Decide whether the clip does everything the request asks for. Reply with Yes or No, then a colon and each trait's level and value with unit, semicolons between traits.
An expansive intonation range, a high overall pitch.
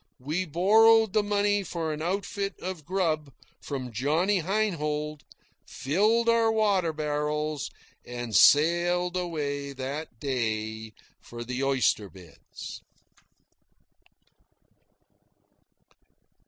No: wide, 5.7 semitones; medium, 155 Hz